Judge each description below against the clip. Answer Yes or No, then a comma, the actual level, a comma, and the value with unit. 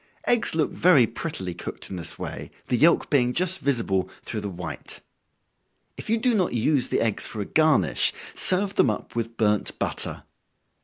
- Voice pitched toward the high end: No, low, 125 Hz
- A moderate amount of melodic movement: No, wide, 8.1 semitones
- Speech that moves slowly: No, average, 175 wpm